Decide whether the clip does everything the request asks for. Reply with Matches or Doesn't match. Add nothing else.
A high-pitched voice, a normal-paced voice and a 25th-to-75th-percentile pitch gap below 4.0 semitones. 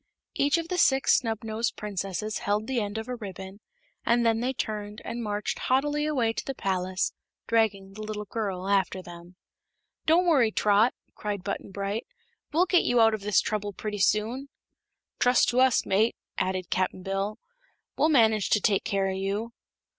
Matches